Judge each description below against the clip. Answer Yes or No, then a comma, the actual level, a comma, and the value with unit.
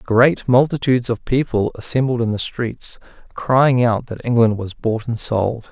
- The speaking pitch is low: Yes, low, 120 Hz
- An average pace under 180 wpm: Yes, average, 170 wpm